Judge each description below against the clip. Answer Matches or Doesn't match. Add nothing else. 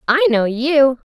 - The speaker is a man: Doesn't match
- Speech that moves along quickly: Doesn't match